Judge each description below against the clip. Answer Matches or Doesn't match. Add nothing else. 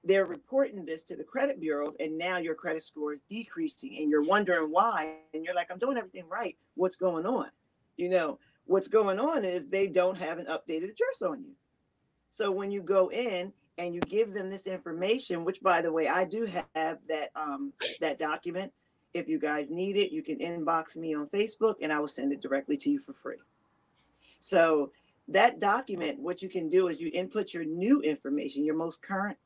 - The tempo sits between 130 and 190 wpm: Doesn't match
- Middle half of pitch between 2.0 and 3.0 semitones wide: Doesn't match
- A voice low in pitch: Doesn't match